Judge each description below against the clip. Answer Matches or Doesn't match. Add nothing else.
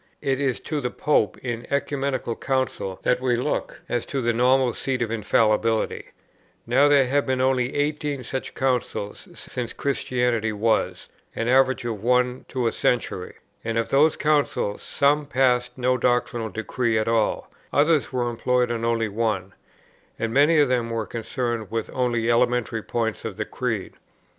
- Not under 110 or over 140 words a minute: Doesn't match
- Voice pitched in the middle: Doesn't match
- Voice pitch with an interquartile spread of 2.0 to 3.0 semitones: Matches